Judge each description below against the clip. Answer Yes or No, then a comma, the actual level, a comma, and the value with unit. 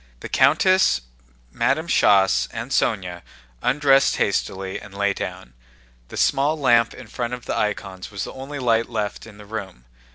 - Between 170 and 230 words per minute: No, average, 160 wpm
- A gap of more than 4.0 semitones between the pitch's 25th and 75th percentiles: Yes, wide, 5.4 semitones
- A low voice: Yes, low, 110 Hz